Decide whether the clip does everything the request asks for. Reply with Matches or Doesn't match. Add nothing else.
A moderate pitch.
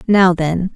Matches